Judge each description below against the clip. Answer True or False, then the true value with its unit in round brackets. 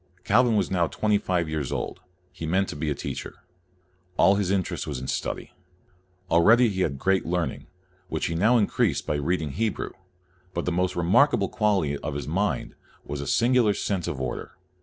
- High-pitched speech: False (90 Hz)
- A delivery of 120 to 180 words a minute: False (195 wpm)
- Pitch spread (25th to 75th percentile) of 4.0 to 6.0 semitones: True (4.7 semitones)